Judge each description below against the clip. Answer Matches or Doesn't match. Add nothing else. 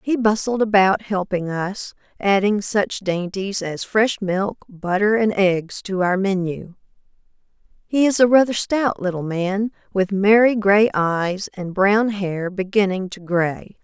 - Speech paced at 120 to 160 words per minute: Matches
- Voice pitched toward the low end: Doesn't match